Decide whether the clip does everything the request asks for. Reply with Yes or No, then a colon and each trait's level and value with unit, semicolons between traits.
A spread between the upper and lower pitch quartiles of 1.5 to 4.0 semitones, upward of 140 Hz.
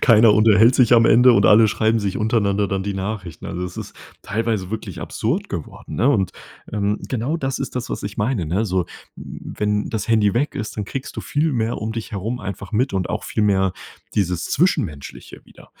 No: average, 2.9 semitones; low, 105 Hz